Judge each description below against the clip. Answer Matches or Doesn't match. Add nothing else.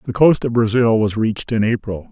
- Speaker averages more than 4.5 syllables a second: Matches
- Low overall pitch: Matches